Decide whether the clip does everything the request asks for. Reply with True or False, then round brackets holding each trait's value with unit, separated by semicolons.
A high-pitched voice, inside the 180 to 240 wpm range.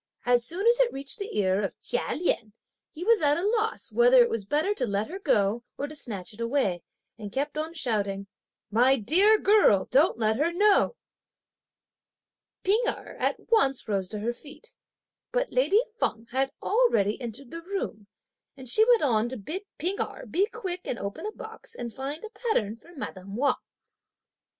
True (280 Hz; 185 wpm)